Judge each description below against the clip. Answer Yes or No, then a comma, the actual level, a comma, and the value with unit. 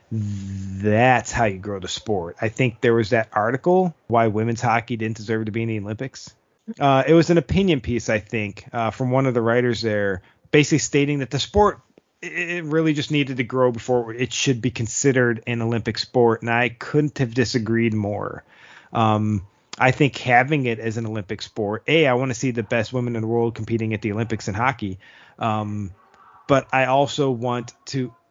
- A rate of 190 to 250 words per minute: Yes, average, 200 wpm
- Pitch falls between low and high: No, low, 120 Hz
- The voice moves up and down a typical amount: Yes, average, 3.1 semitones